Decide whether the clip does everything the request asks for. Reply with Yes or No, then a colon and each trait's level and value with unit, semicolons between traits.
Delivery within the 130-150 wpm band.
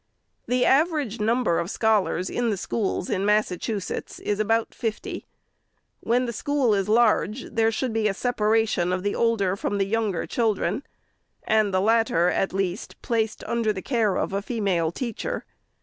No: average, 165 wpm